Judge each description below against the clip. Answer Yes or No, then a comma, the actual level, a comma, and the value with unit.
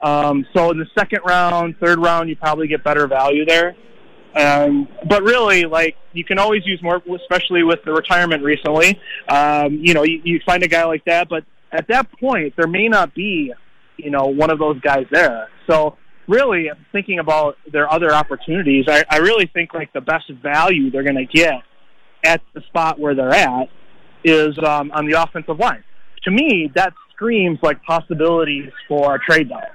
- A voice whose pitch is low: No, medium, 160 Hz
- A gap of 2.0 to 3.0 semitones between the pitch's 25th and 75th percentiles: Yes, average, 2.7 semitones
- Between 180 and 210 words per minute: Yes, average, 190 wpm